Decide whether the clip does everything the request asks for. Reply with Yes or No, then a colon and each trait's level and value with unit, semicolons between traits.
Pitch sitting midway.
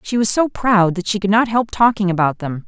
No: high, 205 Hz